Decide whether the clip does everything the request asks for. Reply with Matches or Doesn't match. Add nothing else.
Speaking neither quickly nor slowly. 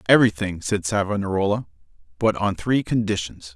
Doesn't match